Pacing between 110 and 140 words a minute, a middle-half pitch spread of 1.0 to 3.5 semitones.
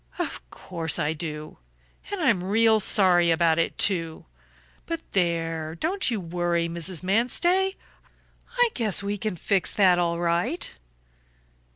No: slow, 135 wpm; average, 4.7 semitones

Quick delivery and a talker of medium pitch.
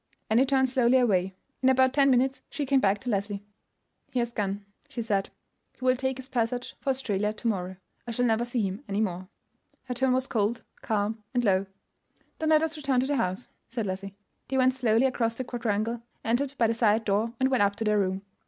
No: fast, 220 wpm; high, 235 Hz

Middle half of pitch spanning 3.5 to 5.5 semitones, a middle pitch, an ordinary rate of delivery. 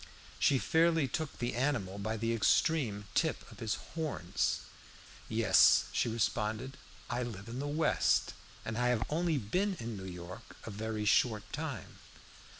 No: average, 5.2 semitones; low, 115 Hz; average, 150 wpm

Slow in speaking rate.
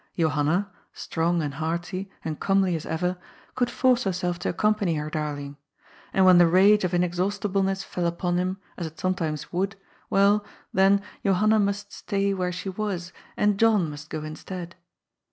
No: average, 160 wpm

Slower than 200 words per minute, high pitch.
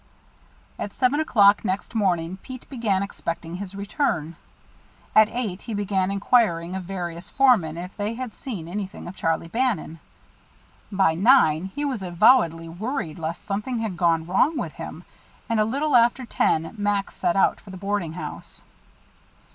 Yes: average, 155 wpm; high, 200 Hz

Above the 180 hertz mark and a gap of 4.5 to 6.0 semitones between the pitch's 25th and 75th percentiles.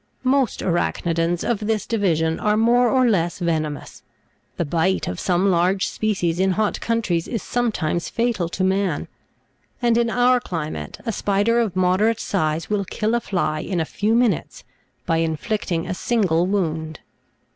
Yes: high, 190 Hz; average, 5.1 semitones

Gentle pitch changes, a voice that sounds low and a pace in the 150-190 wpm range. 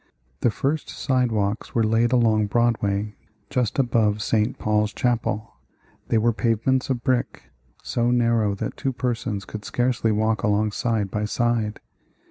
No: narrow, 2.2 semitones; low, 115 Hz; average, 140 wpm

